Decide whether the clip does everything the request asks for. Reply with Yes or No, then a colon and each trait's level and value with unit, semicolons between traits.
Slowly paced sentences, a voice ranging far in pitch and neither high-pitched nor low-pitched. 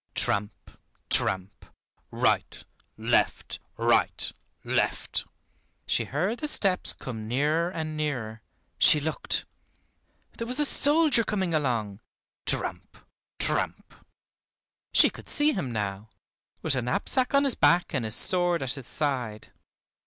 Yes: slow, 125 wpm; wide, 8.5 semitones; medium, 150 Hz